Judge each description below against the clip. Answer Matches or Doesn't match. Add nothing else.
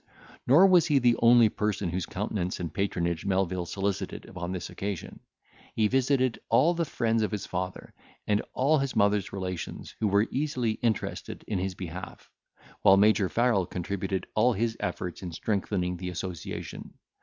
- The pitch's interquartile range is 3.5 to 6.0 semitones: Matches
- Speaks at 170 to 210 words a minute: Doesn't match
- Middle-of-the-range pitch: Doesn't match